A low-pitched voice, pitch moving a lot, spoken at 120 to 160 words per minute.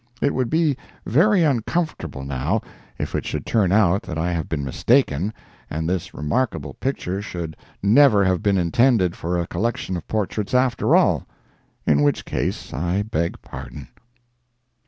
Yes: very low, 95 Hz; wide, 6.8 semitones; average, 150 wpm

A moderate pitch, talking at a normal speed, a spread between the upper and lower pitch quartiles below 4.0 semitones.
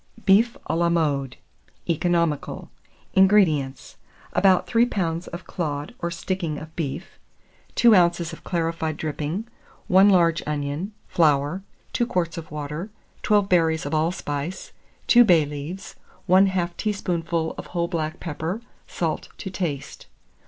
No: medium, 170 Hz; slow, 130 wpm; average, 3.5 semitones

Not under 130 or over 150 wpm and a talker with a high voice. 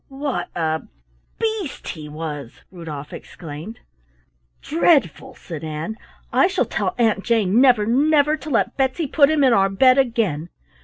Yes: average, 145 wpm; high, 230 Hz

